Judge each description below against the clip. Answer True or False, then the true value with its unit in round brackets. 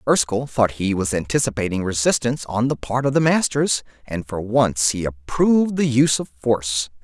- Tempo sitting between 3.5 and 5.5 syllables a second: True (5.3 syllables/s)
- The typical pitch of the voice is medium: False (120 Hz)